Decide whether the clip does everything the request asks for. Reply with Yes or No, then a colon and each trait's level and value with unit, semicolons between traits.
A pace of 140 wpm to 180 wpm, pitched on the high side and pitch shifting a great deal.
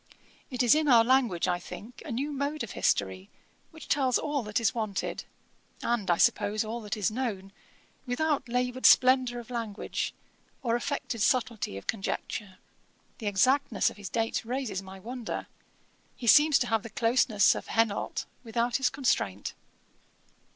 No: average, 160 wpm; high, 235 Hz; average, 3.8 semitones